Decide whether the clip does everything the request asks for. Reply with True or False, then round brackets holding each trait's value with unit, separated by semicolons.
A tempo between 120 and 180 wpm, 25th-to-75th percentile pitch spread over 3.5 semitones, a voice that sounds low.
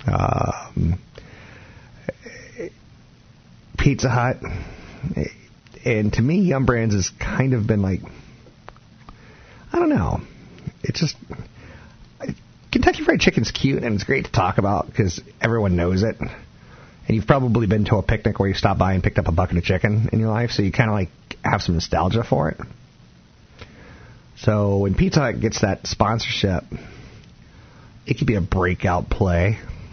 True (150 wpm; 4.2 semitones; 105 Hz)